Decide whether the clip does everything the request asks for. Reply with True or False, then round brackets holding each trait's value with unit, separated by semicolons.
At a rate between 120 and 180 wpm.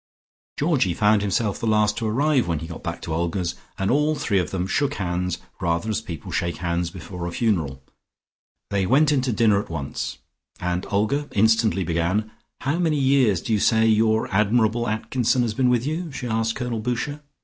False (190 wpm)